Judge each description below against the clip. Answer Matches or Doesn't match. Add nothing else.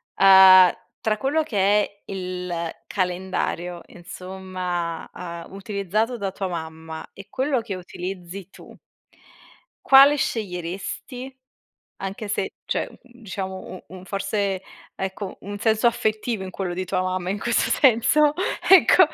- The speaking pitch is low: Doesn't match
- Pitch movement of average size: Matches